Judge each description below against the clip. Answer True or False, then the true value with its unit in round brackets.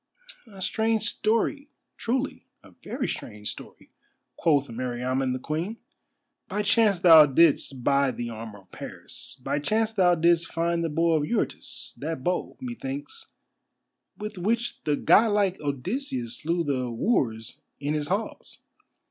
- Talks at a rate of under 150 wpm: True (140 wpm)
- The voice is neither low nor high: True (165 Hz)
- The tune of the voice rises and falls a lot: True (8.0 semitones)